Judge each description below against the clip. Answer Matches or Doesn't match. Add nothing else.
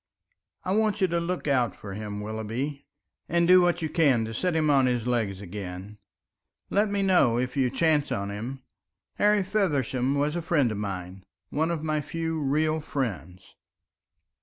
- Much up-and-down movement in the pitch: Matches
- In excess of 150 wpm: Matches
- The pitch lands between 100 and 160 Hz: Matches